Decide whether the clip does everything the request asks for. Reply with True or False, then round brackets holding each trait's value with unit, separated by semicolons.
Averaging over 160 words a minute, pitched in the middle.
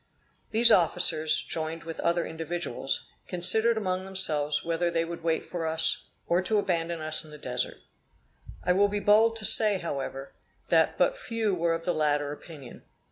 True (170 wpm; 170 Hz)